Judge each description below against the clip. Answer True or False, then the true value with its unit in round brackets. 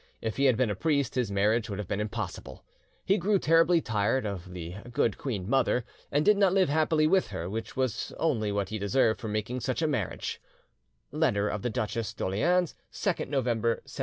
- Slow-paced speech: False (200 wpm)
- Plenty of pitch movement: True (6.2 semitones)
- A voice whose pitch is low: True (115 Hz)